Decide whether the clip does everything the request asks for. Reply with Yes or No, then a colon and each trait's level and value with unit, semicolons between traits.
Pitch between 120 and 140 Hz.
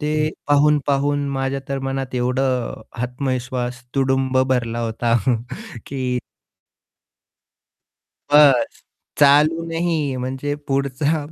Yes: low, 135 Hz